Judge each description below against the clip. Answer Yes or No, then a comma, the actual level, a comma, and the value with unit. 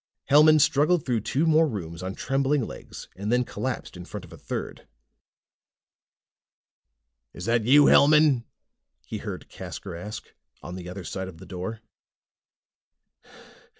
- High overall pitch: No, low, 115 Hz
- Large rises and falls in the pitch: Yes, wide, 7.5 semitones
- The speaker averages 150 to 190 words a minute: No, average, 140 wpm